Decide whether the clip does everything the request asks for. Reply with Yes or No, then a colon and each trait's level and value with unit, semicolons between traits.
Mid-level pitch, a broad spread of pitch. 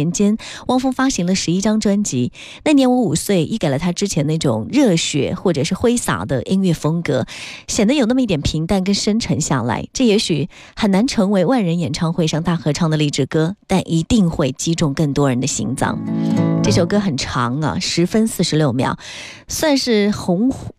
Yes: medium, 175 Hz; wide, 5.8 semitones